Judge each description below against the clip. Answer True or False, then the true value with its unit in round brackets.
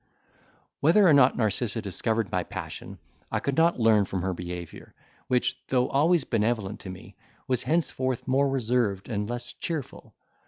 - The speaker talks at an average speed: True (155 wpm)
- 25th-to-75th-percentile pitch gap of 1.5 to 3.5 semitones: False (4.8 semitones)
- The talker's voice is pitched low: True (120 Hz)